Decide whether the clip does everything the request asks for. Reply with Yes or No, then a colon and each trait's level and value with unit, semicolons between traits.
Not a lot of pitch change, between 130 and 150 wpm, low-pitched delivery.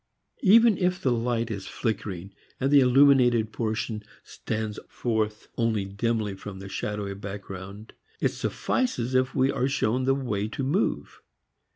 No: average, 4.0 semitones; average, 145 wpm; low, 115 Hz